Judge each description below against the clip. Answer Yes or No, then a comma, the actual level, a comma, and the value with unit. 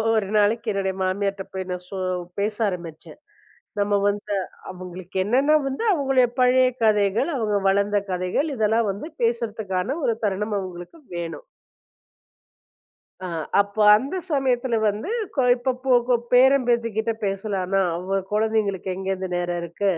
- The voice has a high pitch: Yes, high, 205 Hz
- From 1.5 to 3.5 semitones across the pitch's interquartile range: No, average, 4.1 semitones